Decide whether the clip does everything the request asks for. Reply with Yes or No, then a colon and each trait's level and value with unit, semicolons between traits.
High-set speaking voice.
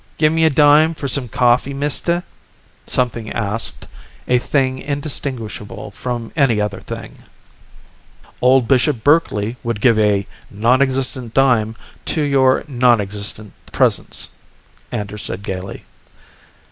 No: low, 125 Hz